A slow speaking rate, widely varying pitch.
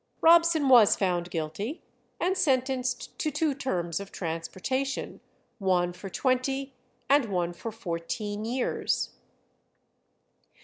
Yes: slow, 105 wpm; wide, 7.2 semitones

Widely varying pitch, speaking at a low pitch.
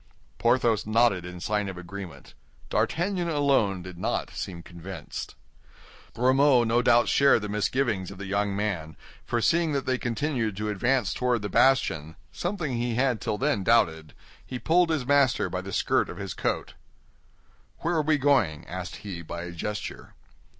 Yes: wide, 6.2 semitones; low, 110 Hz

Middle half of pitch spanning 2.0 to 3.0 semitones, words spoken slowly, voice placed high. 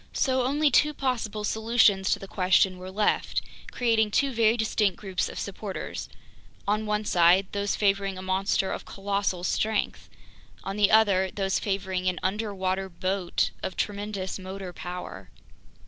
No: narrow, 2.4 semitones; average, 145 wpm; high, 195 Hz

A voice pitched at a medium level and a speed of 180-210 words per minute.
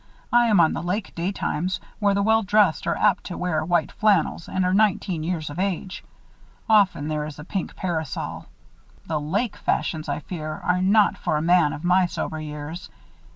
Yes: medium, 180 Hz; average, 190 wpm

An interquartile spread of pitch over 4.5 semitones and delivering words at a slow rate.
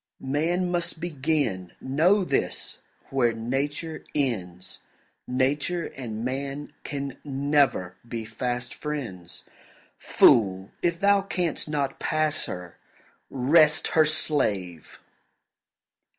Yes: average, 5.3 semitones; slow, 95 wpm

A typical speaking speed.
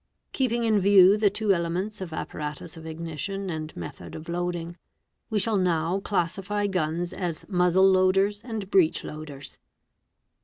Yes: average, 150 wpm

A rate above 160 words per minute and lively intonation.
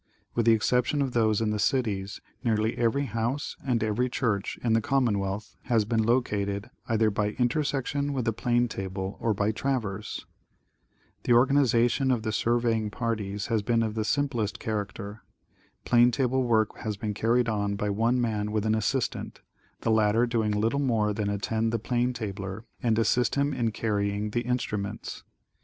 No: average, 170 wpm; narrow, 2.6 semitones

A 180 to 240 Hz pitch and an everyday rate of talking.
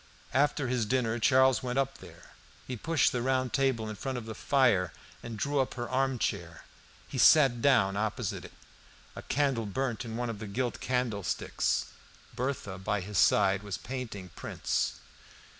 No: low, 120 Hz; average, 165 wpm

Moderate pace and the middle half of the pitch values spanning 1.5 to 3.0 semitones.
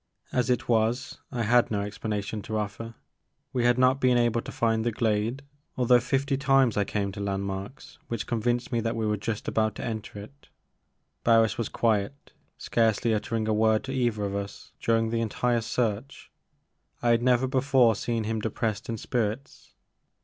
Yes: average, 180 wpm; narrow, 2.4 semitones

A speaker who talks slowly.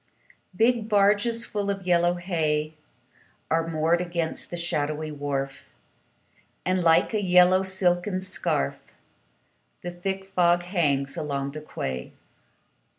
Yes: slow, 115 wpm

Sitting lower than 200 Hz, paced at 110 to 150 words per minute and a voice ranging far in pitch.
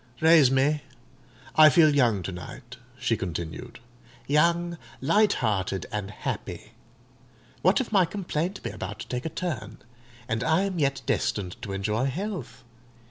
Yes: low, 135 Hz; average, 145 wpm; wide, 7.7 semitones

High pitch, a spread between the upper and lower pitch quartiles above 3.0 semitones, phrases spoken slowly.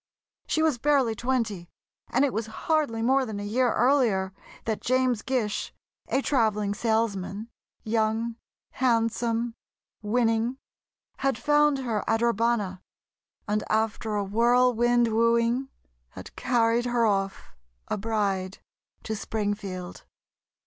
No: high, 230 Hz; average, 2.7 semitones; slow, 110 wpm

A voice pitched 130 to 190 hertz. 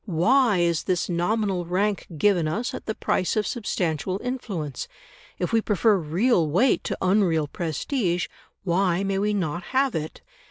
Yes: medium, 185 Hz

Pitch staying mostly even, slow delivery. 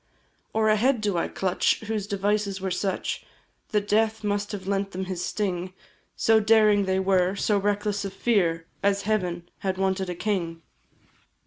No: narrow, 1.9 semitones; average, 165 wpm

